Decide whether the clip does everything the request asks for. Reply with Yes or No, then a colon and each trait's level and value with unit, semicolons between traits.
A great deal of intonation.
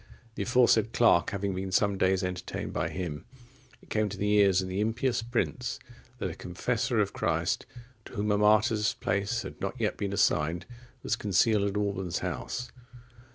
No: average, 2.9 semitones